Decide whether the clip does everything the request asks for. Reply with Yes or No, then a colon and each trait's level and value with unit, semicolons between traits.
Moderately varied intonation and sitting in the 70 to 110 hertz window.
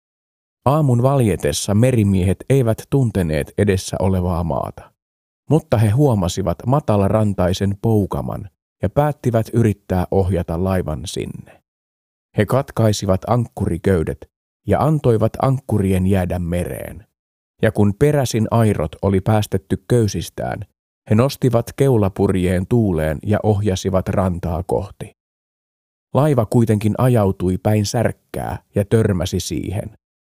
Yes: average, 3.9 semitones; low, 100 Hz